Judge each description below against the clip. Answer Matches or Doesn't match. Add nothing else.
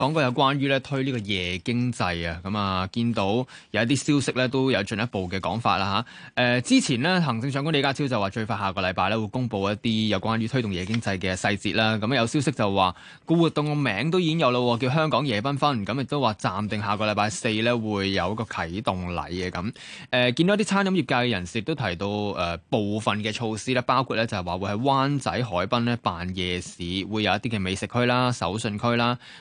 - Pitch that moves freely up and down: Doesn't match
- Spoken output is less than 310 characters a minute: Doesn't match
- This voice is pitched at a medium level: Doesn't match